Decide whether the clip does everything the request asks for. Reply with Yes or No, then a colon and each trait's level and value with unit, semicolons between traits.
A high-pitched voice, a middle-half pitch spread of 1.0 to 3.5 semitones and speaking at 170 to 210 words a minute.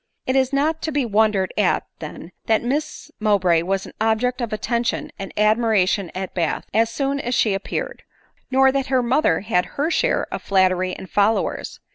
No: high, 220 Hz; average, 5.3 semitones; average, 180 wpm